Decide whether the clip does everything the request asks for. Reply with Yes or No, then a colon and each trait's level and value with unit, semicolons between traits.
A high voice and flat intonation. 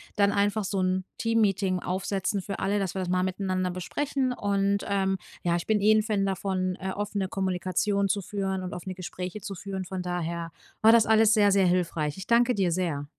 Yes: high, 195 Hz; narrow, 1.9 semitones